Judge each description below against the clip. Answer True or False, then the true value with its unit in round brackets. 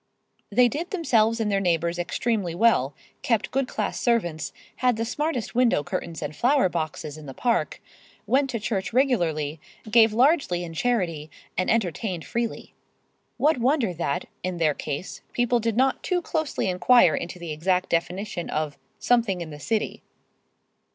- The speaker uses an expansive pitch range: True (6.4 semitones)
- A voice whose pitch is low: False (205 Hz)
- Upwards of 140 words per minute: True (160 wpm)